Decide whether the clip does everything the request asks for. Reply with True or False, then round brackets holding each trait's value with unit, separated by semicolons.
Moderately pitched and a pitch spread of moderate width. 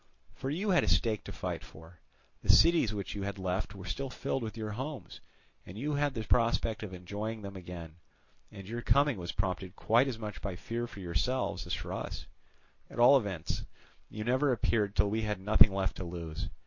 False (105 Hz; 4.2 semitones)